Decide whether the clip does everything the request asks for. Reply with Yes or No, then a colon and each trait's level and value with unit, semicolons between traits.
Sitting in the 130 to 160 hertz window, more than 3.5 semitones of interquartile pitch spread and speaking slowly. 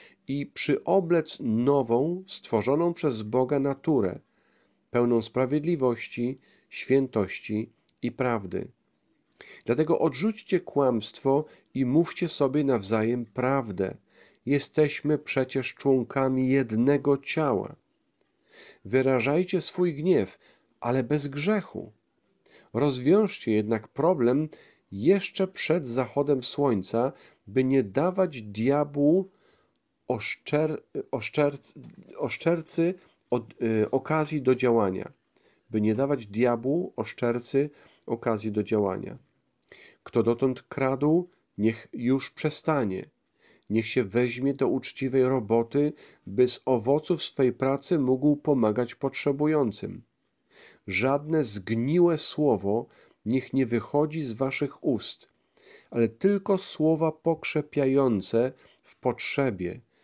Yes: low, 135 Hz; average, 4.1 semitones; slow, 95 wpm